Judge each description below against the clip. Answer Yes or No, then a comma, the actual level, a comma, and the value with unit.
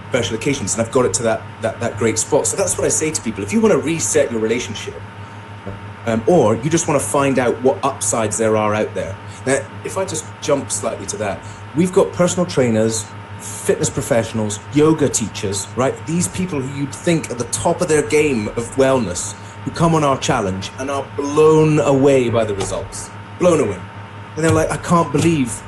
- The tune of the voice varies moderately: No, wide, 5.8 semitones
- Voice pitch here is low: Yes, low, 115 Hz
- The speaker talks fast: Yes, fast, 210 wpm